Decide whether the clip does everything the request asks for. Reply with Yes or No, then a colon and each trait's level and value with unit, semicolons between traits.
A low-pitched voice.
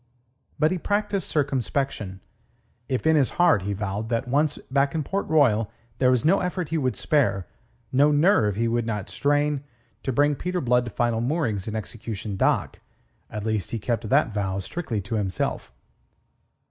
Yes: low, 125 Hz